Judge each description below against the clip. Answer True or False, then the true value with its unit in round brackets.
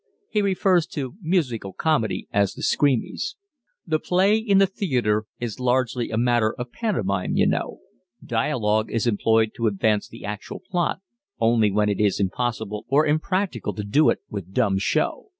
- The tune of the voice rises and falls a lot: True (6.9 semitones)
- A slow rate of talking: False (165 wpm)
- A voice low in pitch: True (120 Hz)